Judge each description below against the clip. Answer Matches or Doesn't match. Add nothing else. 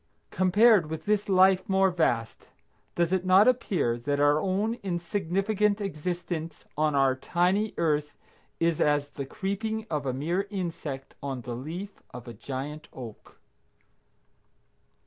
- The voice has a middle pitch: Matches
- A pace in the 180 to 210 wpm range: Doesn't match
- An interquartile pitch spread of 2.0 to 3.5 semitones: Doesn't match